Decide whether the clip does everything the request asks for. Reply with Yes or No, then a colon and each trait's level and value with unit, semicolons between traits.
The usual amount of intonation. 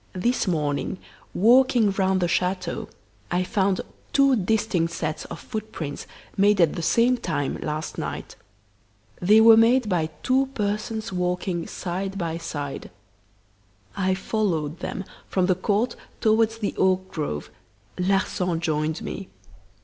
Yes: average, 4.2 semitones